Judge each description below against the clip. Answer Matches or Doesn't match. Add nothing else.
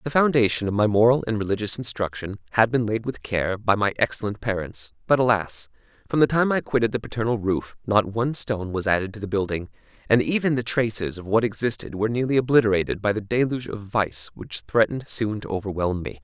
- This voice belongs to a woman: Doesn't match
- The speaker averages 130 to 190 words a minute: Doesn't match